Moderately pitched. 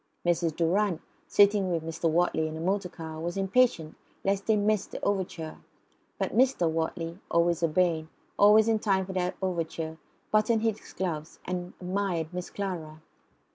Yes: medium, 180 Hz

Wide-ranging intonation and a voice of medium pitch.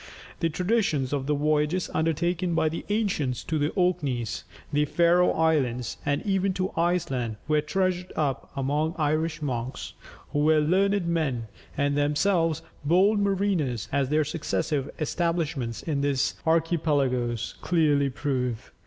No: average, 3.7 semitones; medium, 155 Hz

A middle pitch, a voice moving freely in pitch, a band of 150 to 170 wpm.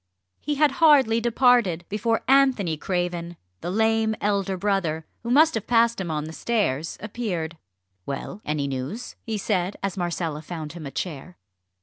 No: high, 195 Hz; wide, 5.7 semitones; average, 155 wpm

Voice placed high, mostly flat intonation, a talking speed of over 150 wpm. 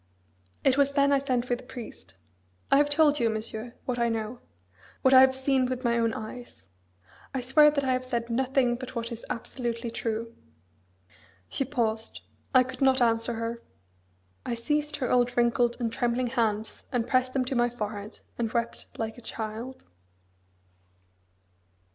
Yes: high, 245 Hz; narrow, 2.2 semitones; average, 170 wpm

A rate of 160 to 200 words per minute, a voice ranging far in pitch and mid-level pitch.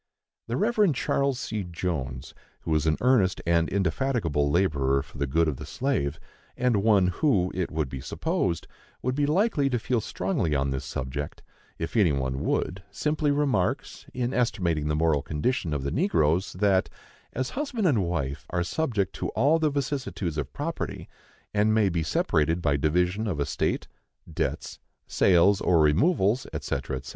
No: average, 165 wpm; wide, 8.7 semitones; very low, 90 Hz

